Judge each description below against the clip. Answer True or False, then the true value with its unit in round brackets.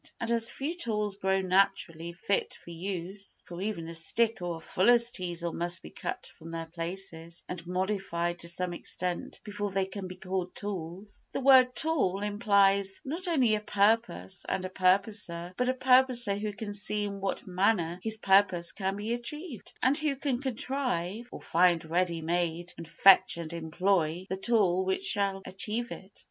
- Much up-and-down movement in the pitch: False (3.8 semitones)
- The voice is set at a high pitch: True (195 Hz)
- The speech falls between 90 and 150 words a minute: False (175 wpm)